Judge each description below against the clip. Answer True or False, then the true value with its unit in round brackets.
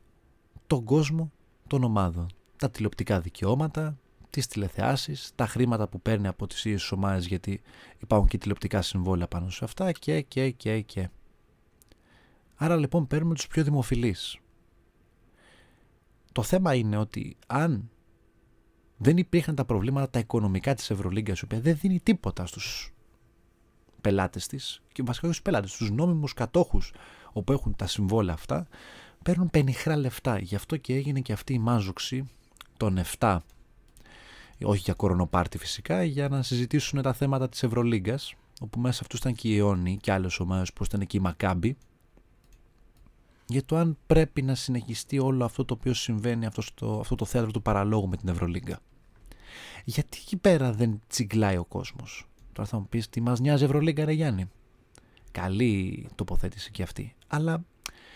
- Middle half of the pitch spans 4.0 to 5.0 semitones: False (5.5 semitones)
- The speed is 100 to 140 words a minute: False (155 wpm)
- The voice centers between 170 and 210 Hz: False (115 Hz)